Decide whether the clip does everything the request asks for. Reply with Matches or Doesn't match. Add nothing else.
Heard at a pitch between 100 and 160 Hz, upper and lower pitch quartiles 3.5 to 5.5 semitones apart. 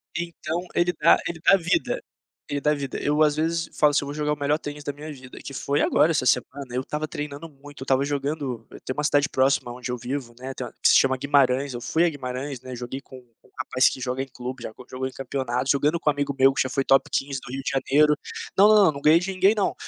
Doesn't match